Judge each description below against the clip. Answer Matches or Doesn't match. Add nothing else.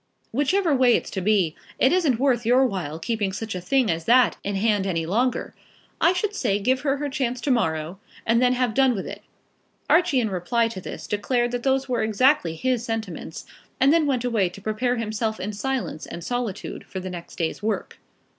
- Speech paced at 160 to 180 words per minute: Doesn't match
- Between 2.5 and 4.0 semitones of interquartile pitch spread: Doesn't match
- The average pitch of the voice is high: Matches